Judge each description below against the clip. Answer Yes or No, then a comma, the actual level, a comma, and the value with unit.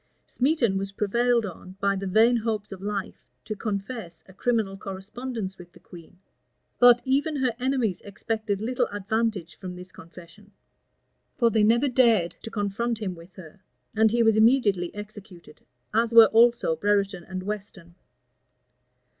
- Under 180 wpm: Yes, average, 150 wpm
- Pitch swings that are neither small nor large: Yes, average, 3.5 semitones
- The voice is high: Yes, high, 210 Hz